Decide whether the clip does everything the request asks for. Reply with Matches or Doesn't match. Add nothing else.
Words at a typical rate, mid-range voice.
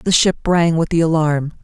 Doesn't match